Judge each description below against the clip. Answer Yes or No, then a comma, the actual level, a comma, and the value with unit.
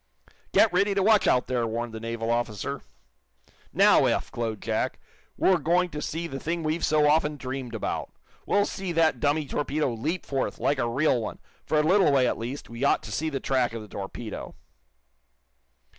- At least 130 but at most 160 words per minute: No, average, 190 wpm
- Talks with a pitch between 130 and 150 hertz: Yes, medium, 140 Hz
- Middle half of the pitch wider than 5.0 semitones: Yes, wide, 5.4 semitones